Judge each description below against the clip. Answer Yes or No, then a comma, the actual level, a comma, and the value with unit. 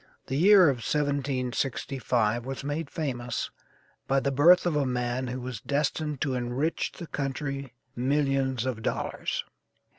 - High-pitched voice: No, low, 135 Hz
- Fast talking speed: No, average, 140 wpm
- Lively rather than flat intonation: No, narrow, 2.6 semitones